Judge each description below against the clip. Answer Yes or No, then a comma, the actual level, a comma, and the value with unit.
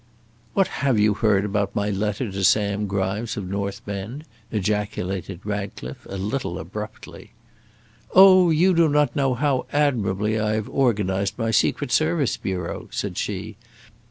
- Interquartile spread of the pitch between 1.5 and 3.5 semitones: No, average, 4.3 semitones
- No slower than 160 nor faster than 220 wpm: No, average, 145 wpm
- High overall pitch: No, low, 105 Hz